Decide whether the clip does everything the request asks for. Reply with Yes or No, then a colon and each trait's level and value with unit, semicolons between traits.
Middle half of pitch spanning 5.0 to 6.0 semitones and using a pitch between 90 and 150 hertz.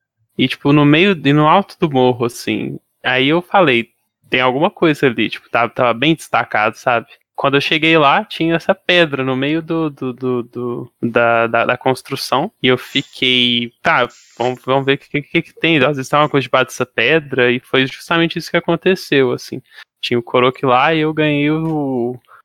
No: average, 4.3 semitones; medium, 140 Hz